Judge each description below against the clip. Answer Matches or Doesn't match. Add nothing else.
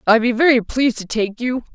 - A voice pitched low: Doesn't match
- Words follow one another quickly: Matches